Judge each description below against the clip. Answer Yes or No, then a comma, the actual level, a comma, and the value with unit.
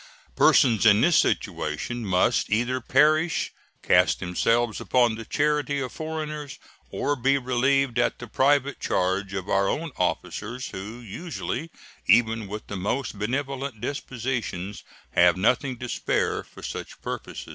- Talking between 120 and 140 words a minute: Yes, slow, 135 wpm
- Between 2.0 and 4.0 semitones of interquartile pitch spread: No, average, 5.0 semitones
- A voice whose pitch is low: Yes, low, 120 Hz